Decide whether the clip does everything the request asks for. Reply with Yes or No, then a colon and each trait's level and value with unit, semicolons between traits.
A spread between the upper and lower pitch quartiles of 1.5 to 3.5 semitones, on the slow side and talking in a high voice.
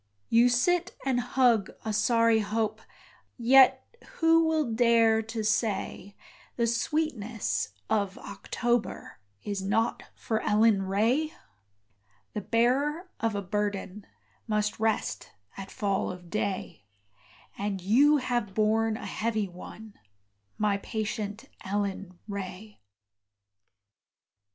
Yes: average, 2.9 semitones; slow, 110 wpm; high, 220 Hz